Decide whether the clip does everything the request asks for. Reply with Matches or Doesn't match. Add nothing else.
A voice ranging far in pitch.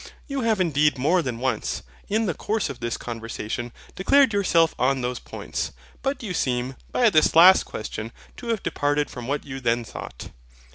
Matches